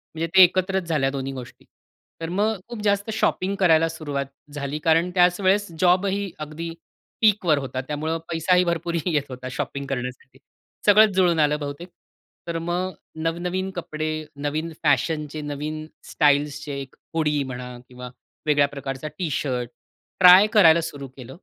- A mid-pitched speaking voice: Yes, medium, 155 Hz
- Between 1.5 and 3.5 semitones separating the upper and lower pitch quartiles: No, average, 4.1 semitones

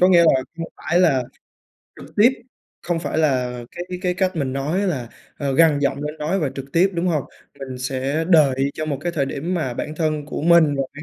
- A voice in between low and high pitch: Yes, medium, 155 Hz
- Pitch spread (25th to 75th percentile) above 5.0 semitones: No, average, 3.8 semitones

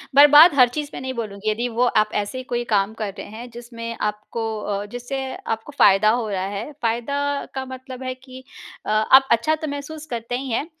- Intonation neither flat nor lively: Yes, average, 3.3 semitones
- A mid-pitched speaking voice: No, high, 240 Hz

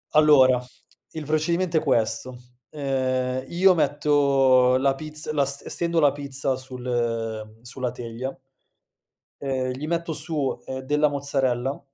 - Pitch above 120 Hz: Yes, low, 135 Hz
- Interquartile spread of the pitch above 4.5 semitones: No, average, 2.9 semitones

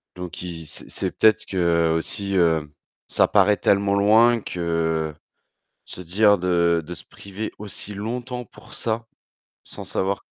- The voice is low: Yes, very low, 95 Hz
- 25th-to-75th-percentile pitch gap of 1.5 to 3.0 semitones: No, average, 3.8 semitones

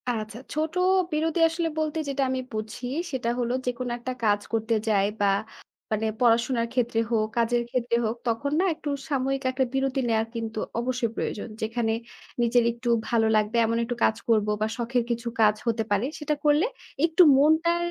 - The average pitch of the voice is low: No, high, 240 Hz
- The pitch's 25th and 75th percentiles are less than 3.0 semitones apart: No, average, 3.3 semitones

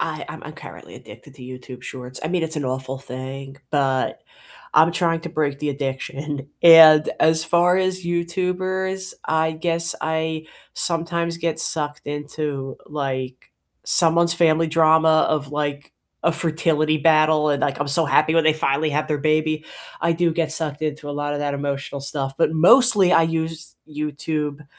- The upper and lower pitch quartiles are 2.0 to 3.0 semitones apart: Yes, narrow, 2.5 semitones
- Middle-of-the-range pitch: Yes, medium, 155 Hz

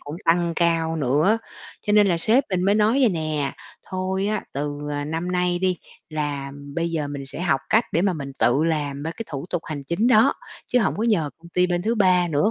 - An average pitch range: Yes, average, 4.5 semitones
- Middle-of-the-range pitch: Yes, medium, 170 Hz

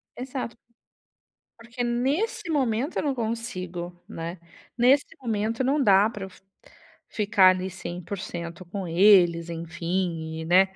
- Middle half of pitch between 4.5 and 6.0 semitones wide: Yes, wide, 5.5 semitones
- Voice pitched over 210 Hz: No, high, 200 Hz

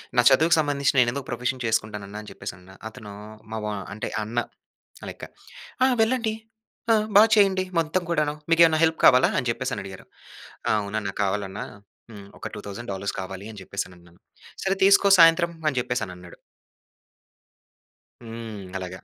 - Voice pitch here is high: No, low, 120 Hz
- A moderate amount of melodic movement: No, wide, 8.1 semitones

